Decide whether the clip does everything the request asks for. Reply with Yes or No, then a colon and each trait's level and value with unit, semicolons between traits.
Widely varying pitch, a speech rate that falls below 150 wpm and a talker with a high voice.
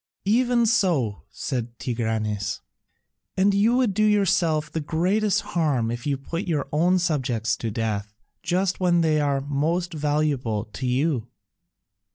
No: wide, 7.3 semitones; average, 140 wpm; medium, 150 Hz